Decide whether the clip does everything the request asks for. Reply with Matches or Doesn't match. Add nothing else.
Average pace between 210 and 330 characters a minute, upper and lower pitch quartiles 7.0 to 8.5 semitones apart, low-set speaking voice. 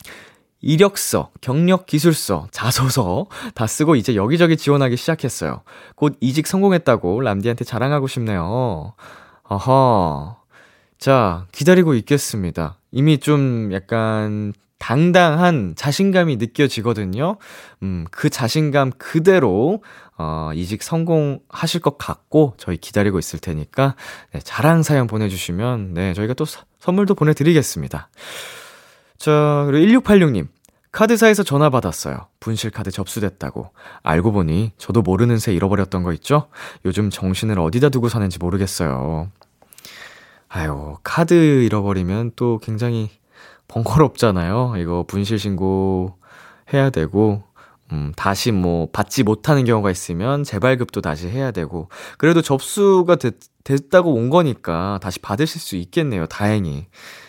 Matches